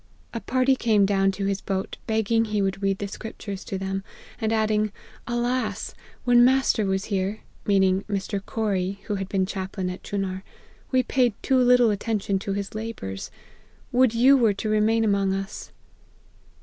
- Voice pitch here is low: No, high, 205 Hz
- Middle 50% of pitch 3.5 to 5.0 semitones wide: No, average, 2.8 semitones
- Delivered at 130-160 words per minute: No, average, 175 wpm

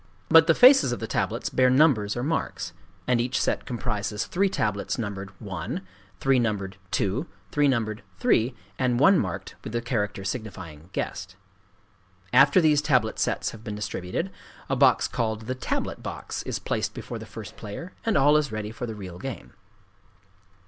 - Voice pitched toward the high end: No, low, 120 Hz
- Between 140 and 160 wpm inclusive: No, average, 170 wpm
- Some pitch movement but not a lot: Yes, average, 4.8 semitones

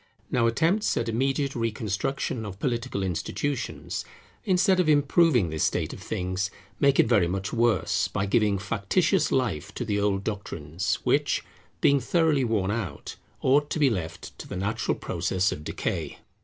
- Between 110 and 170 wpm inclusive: Yes, average, 155 wpm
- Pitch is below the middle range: Yes, low, 115 Hz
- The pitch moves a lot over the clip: Yes, wide, 6.0 semitones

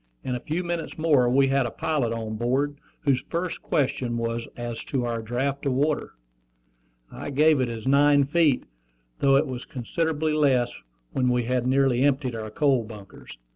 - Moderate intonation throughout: Yes, average, 3.2 semitones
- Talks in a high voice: No, low, 130 Hz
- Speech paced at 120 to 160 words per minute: No, average, 175 wpm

